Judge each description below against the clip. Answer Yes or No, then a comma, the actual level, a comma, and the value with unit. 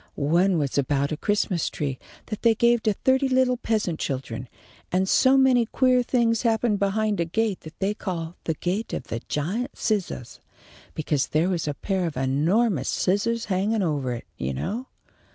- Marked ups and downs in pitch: Yes, wide, 6.8 semitones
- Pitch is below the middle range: No, high, 190 Hz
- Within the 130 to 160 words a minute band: No, average, 175 wpm